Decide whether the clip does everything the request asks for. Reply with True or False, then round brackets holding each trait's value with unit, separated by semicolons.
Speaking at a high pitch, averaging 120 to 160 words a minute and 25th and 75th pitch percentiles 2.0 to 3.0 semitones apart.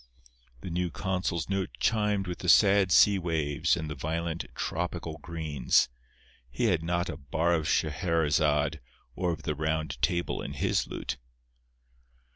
False (85 Hz; 140 wpm; 2.6 semitones)